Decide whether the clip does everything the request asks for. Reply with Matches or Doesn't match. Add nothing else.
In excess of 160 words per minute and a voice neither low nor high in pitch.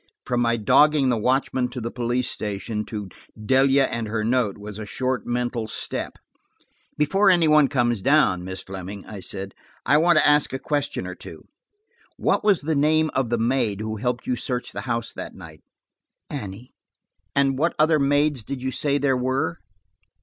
Doesn't match